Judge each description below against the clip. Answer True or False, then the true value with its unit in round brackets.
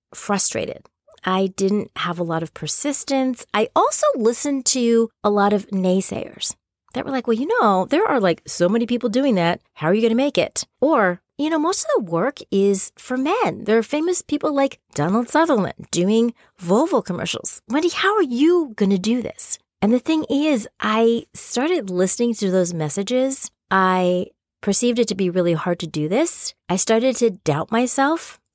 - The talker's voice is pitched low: False (230 Hz)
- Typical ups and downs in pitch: False (6.2 semitones)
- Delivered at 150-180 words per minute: False (190 wpm)